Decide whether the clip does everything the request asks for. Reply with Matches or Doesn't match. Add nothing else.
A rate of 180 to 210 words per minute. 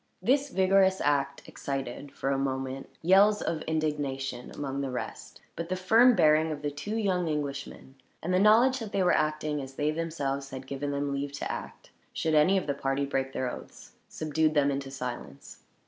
Matches